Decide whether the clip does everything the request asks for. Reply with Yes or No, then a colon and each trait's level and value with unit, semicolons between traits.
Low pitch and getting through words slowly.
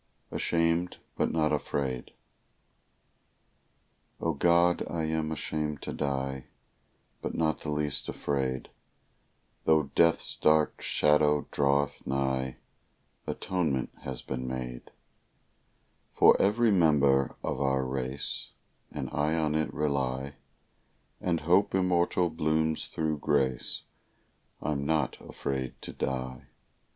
Yes: very low, 75 Hz; slow, 105 wpm